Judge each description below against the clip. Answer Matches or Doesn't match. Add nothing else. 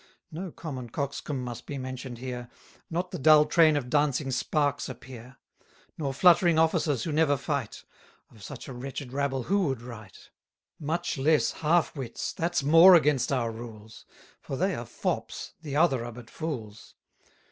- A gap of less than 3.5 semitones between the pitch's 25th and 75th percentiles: Doesn't match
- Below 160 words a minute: Doesn't match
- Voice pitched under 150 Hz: Matches